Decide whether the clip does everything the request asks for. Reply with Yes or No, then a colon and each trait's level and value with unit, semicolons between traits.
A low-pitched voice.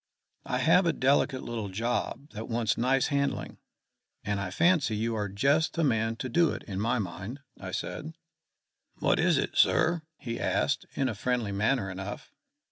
Yes: low, 120 Hz